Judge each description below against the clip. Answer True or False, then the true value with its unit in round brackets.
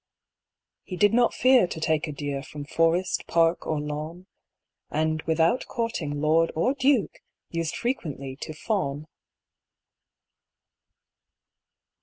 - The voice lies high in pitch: False (165 Hz)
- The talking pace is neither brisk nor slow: False (115 wpm)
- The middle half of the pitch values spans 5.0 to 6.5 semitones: False (4.1 semitones)